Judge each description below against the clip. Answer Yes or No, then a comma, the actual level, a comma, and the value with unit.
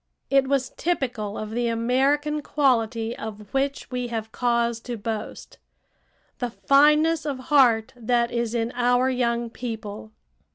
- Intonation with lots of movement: No, average, 2.9 semitones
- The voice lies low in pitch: No, high, 240 Hz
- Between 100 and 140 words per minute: Yes, slow, 135 wpm